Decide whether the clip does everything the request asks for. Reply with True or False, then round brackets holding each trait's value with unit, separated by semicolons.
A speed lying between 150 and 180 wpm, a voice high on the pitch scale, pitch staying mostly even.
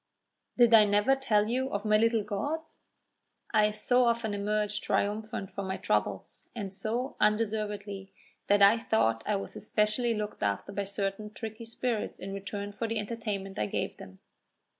True (160 wpm; 210 Hz; 2.1 semitones)